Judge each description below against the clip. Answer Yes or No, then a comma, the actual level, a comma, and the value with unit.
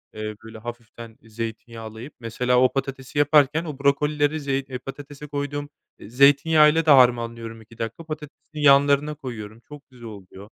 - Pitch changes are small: No, average, 4.1 semitones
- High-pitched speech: No, low, 135 Hz